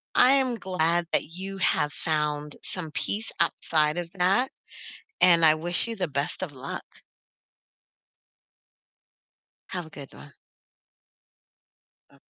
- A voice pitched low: No, medium, 170 Hz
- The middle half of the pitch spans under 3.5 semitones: No, average, 3.9 semitones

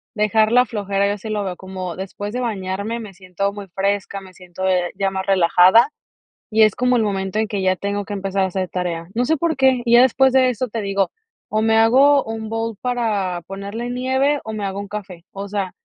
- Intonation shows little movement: No, average, 3.2 semitones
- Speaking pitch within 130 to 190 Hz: No, high, 205 Hz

